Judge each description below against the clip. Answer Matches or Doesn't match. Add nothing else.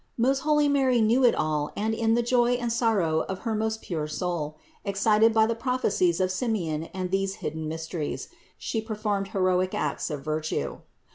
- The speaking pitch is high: Matches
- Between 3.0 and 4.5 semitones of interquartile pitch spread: Doesn't match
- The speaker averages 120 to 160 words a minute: Doesn't match